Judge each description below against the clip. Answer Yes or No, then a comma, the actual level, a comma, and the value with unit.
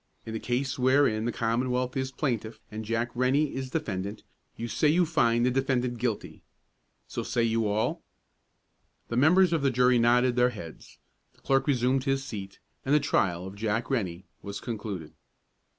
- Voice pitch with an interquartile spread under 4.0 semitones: Yes, average, 3.4 semitones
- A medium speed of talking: Yes, average, 170 wpm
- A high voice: No, low, 120 Hz